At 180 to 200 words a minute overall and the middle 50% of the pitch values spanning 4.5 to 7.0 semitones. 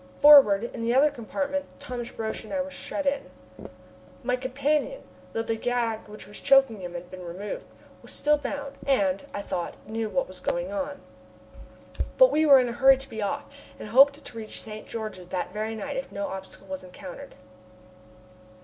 Yes: average, 185 wpm; wide, 5.5 semitones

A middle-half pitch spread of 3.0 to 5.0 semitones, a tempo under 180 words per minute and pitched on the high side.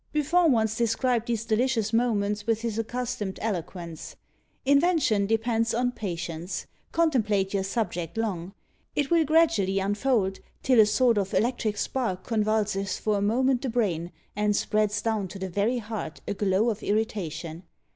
Yes: average, 3.5 semitones; average, 150 wpm; high, 215 Hz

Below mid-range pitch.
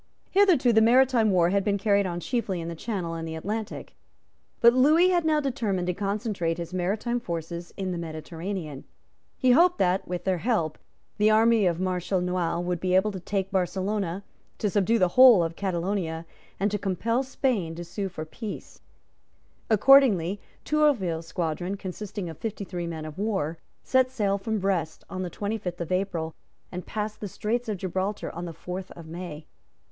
No: high, 190 Hz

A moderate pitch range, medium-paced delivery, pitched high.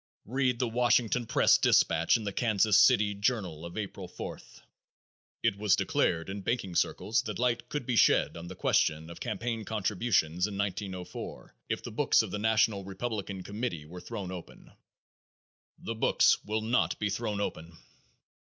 No: average, 3.8 semitones; average, 160 wpm; low, 105 Hz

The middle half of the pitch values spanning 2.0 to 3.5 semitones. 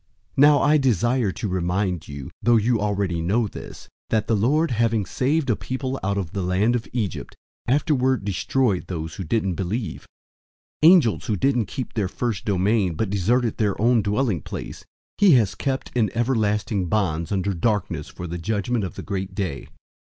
No: average, 4.4 semitones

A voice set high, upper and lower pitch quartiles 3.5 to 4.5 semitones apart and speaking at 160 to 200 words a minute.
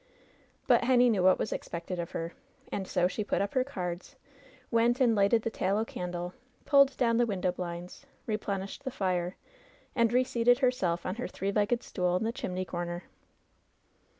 No: high, 200 Hz; average, 4.9 semitones; average, 175 wpm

